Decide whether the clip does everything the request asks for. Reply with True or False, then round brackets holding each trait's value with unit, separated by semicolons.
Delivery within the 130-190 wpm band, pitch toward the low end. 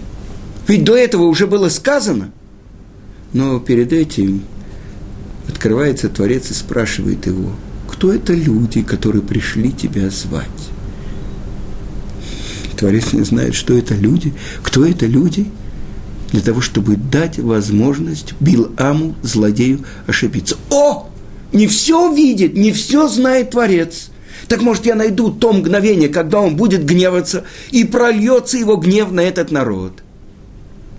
False (120 wpm; 130 Hz)